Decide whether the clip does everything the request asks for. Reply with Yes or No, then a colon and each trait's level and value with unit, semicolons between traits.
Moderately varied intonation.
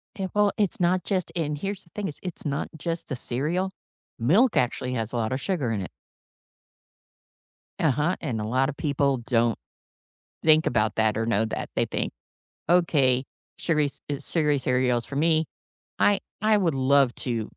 No: wide, 5.8 semitones